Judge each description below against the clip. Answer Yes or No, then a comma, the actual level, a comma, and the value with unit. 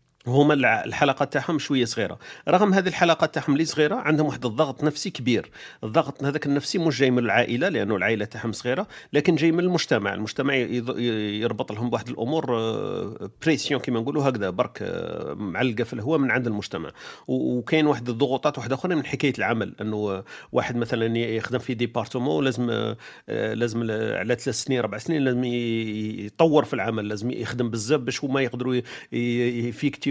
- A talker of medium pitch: No, low, 125 Hz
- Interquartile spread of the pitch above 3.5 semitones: Yes, average, 4.0 semitones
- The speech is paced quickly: Yes, fast, 160 wpm